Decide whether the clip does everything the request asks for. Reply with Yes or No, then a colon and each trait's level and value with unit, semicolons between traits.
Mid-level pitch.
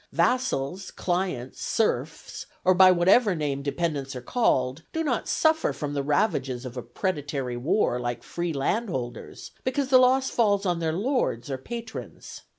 Yes: medium, 170 Hz